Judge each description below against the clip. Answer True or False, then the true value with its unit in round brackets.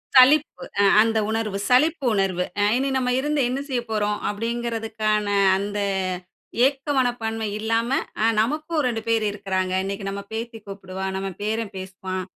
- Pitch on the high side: True (225 Hz)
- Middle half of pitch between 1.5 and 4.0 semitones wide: True (3.7 semitones)